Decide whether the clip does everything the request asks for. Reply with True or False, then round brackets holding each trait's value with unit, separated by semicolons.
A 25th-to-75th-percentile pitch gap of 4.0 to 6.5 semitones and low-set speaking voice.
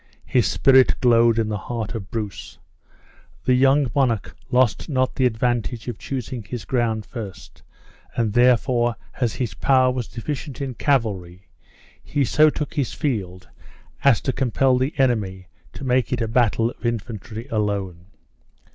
False (3.0 semitones; 120 Hz)